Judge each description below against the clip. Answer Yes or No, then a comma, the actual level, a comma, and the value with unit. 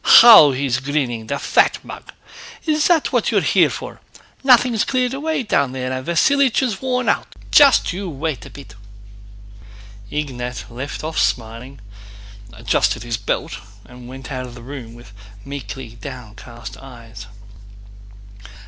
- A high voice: No, low, 135 Hz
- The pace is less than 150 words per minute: Yes, average, 140 wpm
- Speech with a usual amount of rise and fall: No, wide, 9.0 semitones